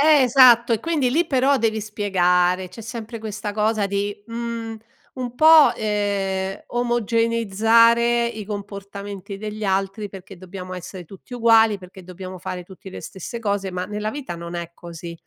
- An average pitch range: Yes, average, 3.4 semitones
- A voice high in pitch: Yes, high, 210 Hz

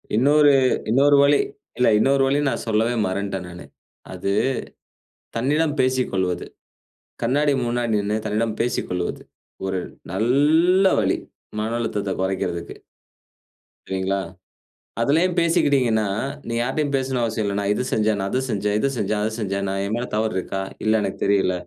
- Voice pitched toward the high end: No, low, 110 Hz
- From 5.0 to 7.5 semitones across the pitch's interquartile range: Yes, average, 5.3 semitones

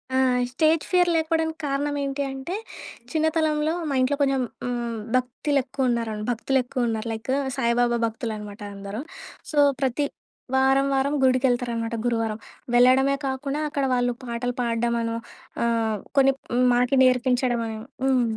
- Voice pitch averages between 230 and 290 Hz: Yes, very high, 255 Hz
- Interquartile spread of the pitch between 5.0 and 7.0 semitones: No, average, 2.8 semitones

